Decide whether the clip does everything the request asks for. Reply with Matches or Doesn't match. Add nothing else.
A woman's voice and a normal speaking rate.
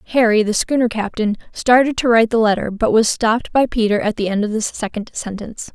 Doesn't match